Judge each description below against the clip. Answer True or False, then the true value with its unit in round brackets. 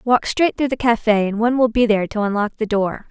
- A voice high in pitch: True (225 Hz)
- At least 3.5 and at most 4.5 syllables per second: False (6.0 syllables/s)